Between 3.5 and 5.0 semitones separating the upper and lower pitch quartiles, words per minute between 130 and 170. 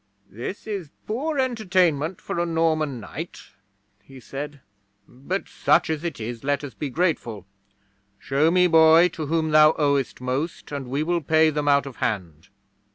Yes: average, 3.9 semitones; average, 160 wpm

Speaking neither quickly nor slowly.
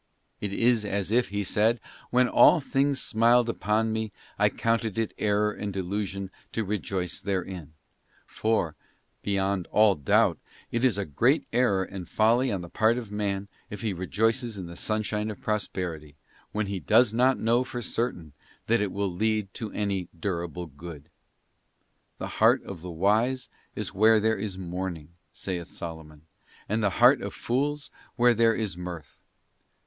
Yes: average, 165 wpm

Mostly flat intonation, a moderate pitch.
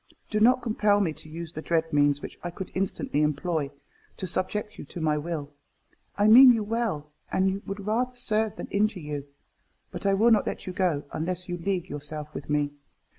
No: wide, 5.6 semitones; medium, 180 Hz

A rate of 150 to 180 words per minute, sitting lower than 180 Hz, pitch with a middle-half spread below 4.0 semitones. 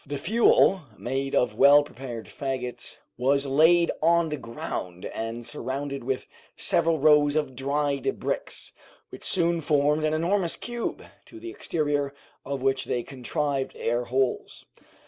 No: average, 140 wpm; medium, 140 Hz; average, 3.0 semitones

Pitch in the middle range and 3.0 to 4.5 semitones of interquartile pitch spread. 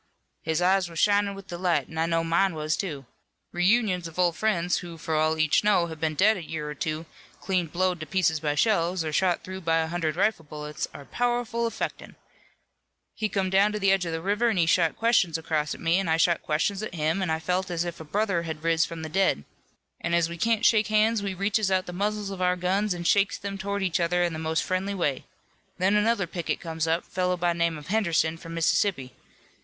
Yes: medium, 175 Hz; average, 3.4 semitones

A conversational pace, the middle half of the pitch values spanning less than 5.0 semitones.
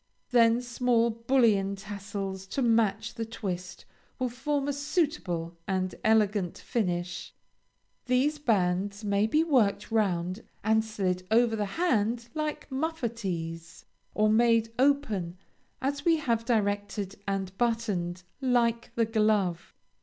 No: slow, 120 wpm; average, 3.9 semitones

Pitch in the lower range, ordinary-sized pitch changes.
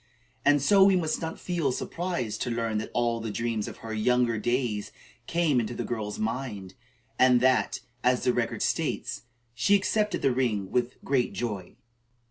Yes: low, 120 Hz; average, 3.8 semitones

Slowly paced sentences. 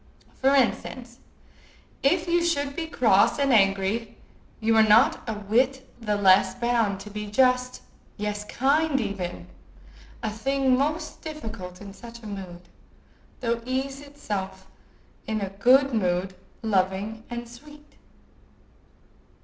Yes: slow, 120 wpm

